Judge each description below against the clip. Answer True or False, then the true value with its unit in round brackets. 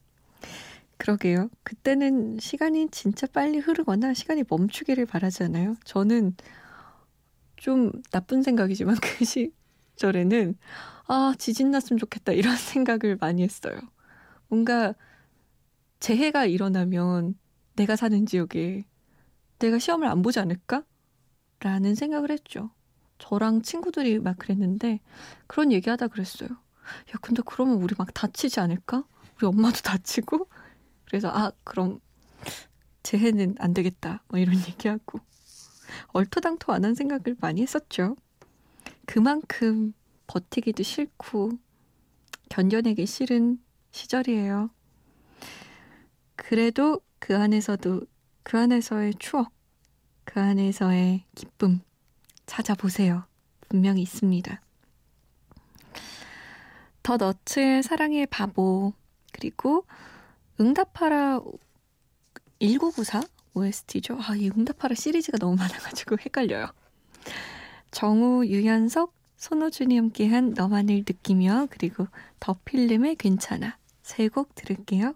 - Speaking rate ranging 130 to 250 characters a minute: True (245 characters per minute)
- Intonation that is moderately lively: True (4.7 semitones)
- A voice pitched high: True (220 Hz)